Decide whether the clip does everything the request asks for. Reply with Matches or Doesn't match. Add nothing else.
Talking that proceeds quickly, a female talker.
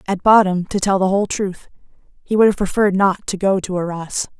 Matches